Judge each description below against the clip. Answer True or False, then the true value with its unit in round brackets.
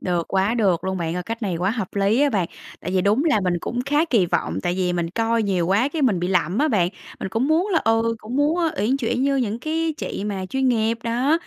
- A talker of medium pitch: False (225 Hz)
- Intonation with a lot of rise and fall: True (6.2 semitones)